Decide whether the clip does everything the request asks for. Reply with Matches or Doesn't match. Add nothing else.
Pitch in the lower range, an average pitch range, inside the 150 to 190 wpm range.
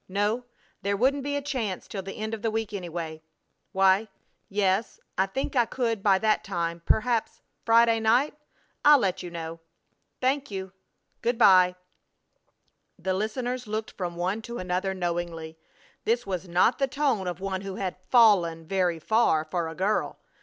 Doesn't match